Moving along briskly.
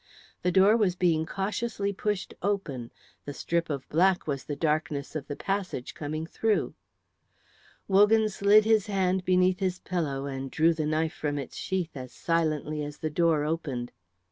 No: average, 165 wpm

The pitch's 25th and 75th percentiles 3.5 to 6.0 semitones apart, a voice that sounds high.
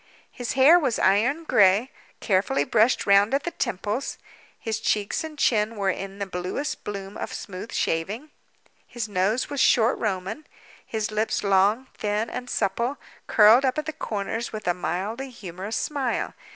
Yes: average, 4.3 semitones; high, 215 Hz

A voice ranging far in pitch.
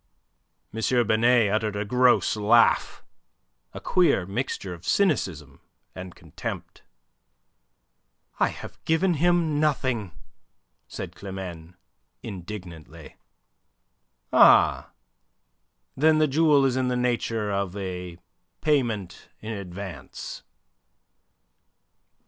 Yes: wide, 6.2 semitones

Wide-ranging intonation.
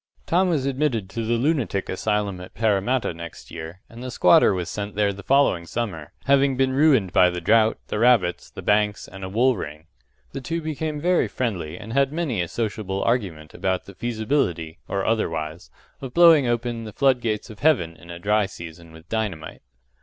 Yes: wide, 6.3 semitones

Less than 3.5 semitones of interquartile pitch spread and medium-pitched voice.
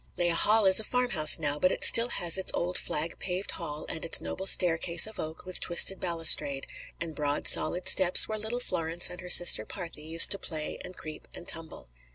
Yes: average, 2.9 semitones; medium, 175 Hz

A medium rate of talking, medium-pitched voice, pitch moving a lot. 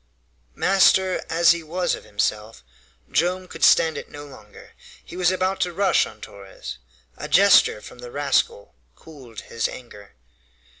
Yes: average, 150 wpm; medium, 145 Hz; wide, 8.8 semitones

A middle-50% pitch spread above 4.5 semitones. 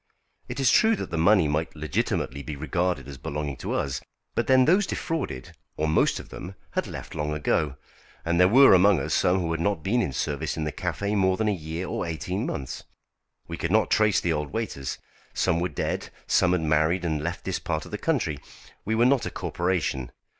Yes: average, 5.0 semitones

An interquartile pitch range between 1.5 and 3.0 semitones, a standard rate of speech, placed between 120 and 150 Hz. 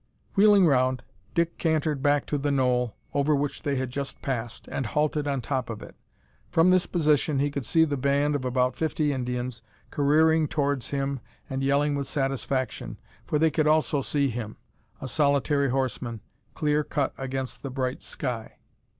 Yes: narrow, 2.5 semitones; average, 175 wpm; medium, 140 Hz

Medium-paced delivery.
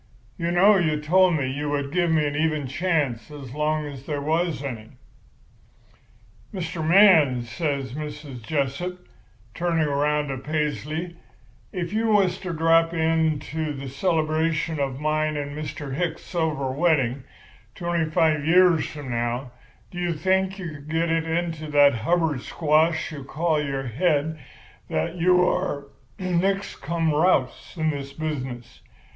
Yes: average, 150 wpm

